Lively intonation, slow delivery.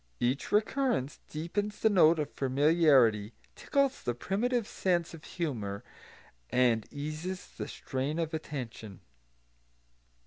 Yes: wide, 6.5 semitones; slow, 110 wpm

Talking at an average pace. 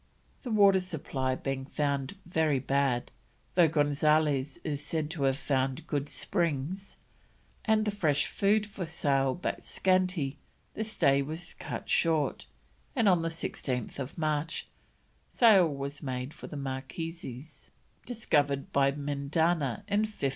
No: slow, 130 wpm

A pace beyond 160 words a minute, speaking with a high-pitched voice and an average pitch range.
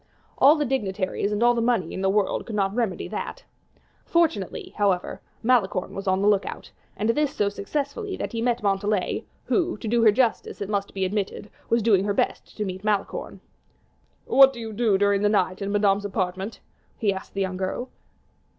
Yes: average, 195 wpm; high, 205 Hz; average, 3.3 semitones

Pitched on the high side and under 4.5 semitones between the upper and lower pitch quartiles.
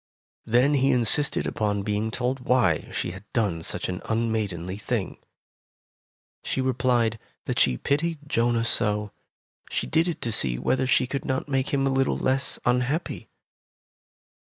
No: low, 120 Hz; average, 4.1 semitones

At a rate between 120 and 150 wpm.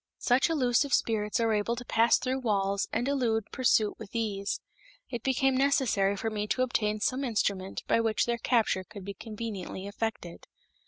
No: average, 170 wpm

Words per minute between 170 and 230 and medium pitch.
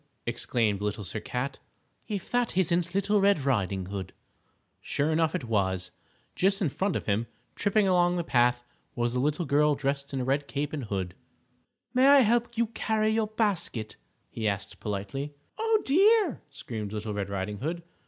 Yes: average, 175 wpm; medium, 145 Hz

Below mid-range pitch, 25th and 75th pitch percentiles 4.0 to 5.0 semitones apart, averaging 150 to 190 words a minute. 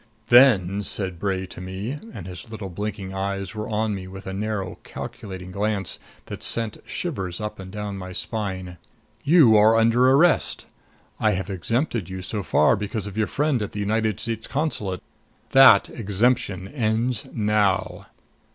No: low, 105 Hz; average, 2.9 semitones; average, 160 wpm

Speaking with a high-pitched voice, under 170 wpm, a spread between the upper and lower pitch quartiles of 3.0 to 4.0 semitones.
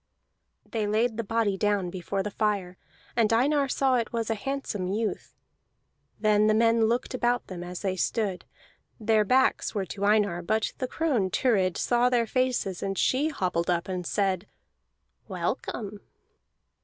Yes: high, 215 Hz; average, 155 wpm; average, 3.6 semitones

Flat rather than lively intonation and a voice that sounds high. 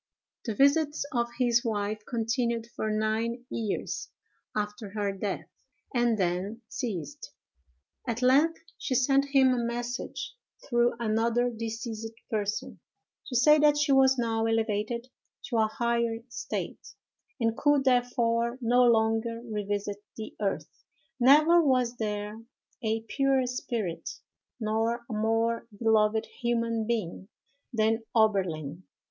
Yes: narrow, 2.2 semitones; high, 230 Hz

